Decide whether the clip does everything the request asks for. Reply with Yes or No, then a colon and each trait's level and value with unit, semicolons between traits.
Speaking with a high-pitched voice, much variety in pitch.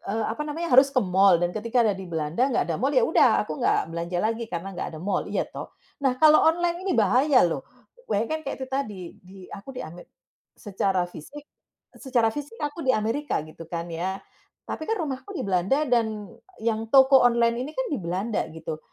Yes: high, 230 Hz; wide, 7.0 semitones